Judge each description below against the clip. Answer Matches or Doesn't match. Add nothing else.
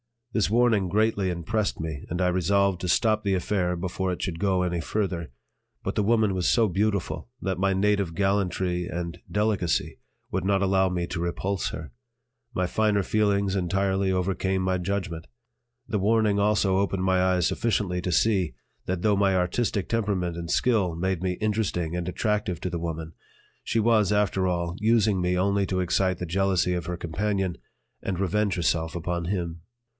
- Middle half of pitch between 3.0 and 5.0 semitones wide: Doesn't match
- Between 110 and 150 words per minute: Doesn't match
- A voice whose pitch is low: Matches